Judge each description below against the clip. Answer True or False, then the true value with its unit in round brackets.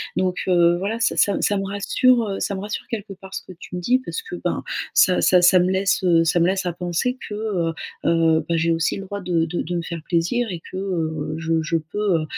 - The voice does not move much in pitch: False (3.0 semitones)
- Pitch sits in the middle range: True (180 Hz)